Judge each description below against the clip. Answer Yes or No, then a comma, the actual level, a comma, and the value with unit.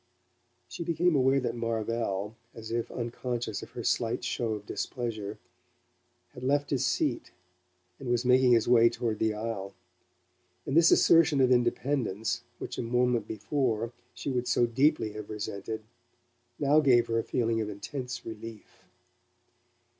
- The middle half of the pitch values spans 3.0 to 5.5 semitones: No, narrow, 2.6 semitones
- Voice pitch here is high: No, low, 120 Hz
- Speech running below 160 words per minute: Yes, average, 145 wpm